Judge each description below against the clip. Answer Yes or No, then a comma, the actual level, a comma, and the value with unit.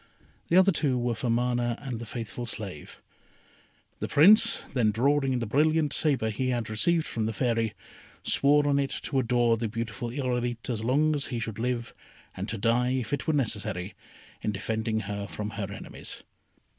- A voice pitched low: Yes, low, 120 Hz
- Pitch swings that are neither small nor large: Yes, average, 3.7 semitones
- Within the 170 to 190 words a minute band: Yes, average, 180 wpm